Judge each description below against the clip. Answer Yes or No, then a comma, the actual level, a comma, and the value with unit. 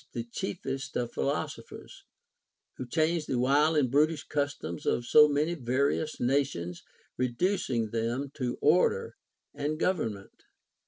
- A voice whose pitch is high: No, medium, 140 Hz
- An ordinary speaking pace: No, slow, 125 wpm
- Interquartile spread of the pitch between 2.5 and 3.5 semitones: No, average, 4.2 semitones